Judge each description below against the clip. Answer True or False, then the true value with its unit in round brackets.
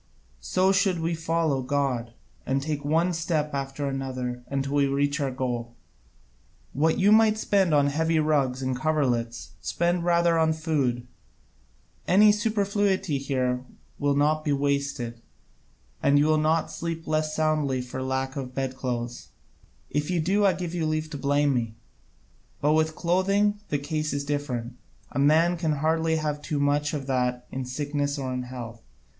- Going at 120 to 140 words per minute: False (160 wpm)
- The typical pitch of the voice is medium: True (145 Hz)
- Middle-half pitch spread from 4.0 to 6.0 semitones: False (3.5 semitones)